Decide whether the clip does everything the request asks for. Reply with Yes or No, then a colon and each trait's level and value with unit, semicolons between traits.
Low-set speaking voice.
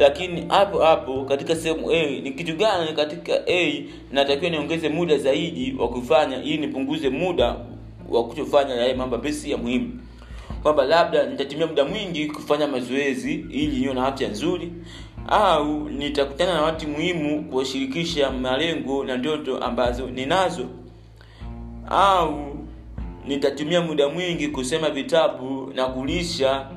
No: medium, 145 Hz